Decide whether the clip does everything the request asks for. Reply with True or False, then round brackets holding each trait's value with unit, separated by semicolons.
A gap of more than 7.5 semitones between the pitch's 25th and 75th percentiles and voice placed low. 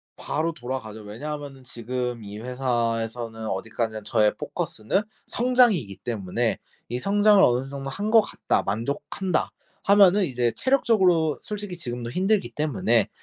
True (8.3 semitones; 130 Hz)